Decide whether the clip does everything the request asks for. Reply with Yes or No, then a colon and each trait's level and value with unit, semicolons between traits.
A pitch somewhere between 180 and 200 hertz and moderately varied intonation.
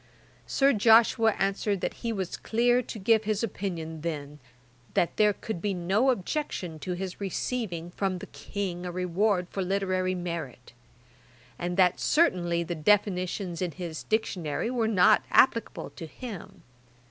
Yes: high, 190 Hz; average, 3.9 semitones